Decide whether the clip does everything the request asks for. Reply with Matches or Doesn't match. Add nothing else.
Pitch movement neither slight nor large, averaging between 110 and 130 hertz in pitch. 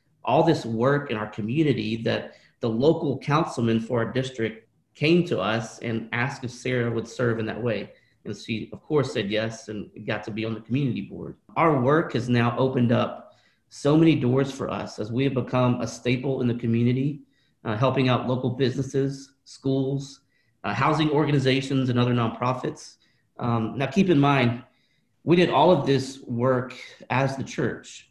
Matches